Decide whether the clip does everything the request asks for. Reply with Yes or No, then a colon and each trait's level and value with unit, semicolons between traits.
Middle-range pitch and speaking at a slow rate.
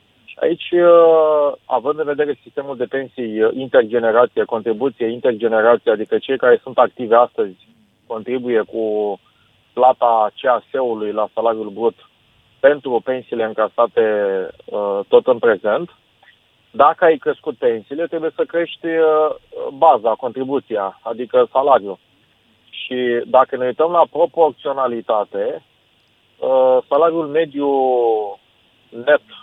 Yes: medium, 150 Hz; slow, 100 wpm